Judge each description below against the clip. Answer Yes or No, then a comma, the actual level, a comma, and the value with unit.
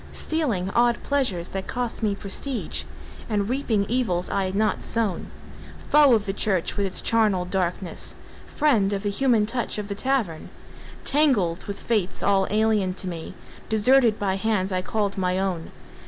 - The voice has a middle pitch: No, high, 205 Hz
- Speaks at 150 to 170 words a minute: Yes, average, 165 wpm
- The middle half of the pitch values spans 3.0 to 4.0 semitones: Yes, average, 3.7 semitones